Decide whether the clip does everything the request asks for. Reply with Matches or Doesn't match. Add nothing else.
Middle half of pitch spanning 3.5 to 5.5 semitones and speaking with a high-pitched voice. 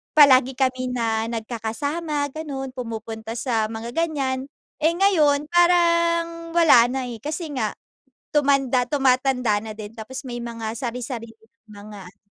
Matches